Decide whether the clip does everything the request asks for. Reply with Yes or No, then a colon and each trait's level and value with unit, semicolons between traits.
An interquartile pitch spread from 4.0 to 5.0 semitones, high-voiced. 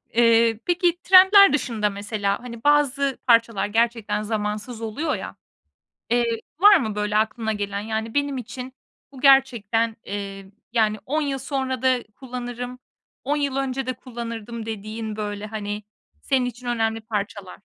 No: average, 3.5 semitones; high, 230 Hz